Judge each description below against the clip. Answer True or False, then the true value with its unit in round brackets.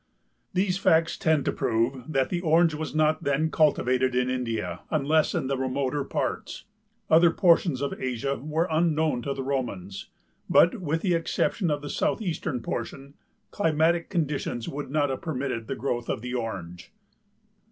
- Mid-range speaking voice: True (145 Hz)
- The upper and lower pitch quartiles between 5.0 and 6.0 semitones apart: False (3.8 semitones)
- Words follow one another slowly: False (160 wpm)